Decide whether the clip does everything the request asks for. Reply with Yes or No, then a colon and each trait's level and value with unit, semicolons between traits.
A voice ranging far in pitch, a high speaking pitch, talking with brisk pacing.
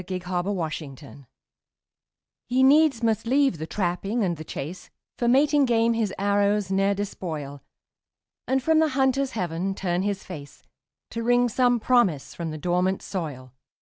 No: wide, 5.8 semitones; high, 200 Hz; average, 155 wpm